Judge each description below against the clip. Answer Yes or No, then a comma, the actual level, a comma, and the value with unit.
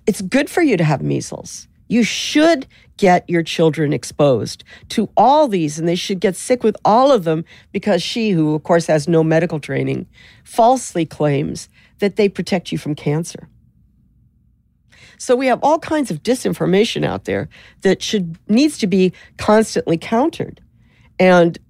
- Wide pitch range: Yes, wide, 6.4 semitones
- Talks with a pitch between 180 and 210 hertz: Yes, high, 190 Hz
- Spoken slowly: No, average, 165 wpm